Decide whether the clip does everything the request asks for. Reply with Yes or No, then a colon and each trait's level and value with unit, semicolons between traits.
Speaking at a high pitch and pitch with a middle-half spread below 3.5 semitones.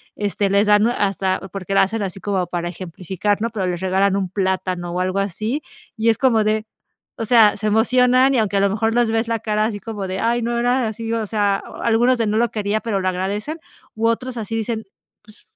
Yes: high, 210 Hz; average, 2.8 semitones